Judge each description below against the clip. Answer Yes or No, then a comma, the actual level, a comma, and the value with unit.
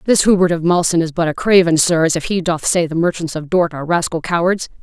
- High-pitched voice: No, medium, 170 Hz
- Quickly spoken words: Yes, fast, 250 wpm